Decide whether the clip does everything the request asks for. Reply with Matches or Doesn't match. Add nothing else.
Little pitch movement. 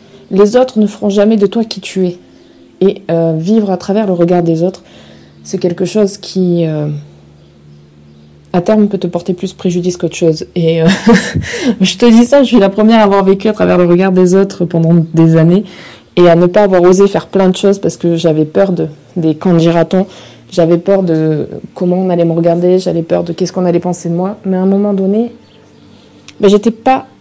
Doesn't match